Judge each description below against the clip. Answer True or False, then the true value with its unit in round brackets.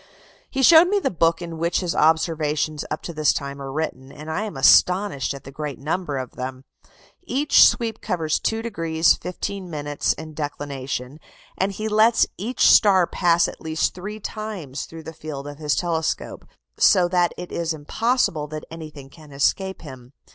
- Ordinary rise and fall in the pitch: True (4.6 semitones)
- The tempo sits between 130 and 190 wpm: True (170 wpm)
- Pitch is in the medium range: True (160 Hz)